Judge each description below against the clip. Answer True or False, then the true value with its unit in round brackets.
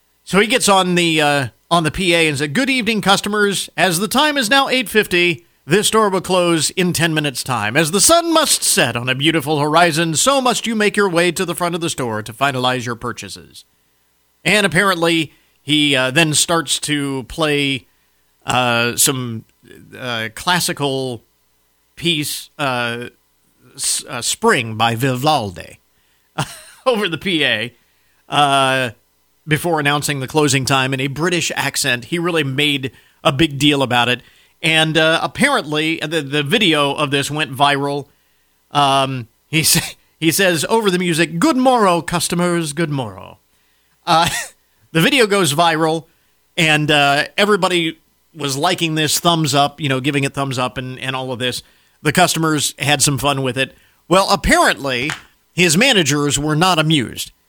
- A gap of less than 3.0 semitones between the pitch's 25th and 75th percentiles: False (5.2 semitones)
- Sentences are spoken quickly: False (160 wpm)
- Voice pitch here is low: False (150 Hz)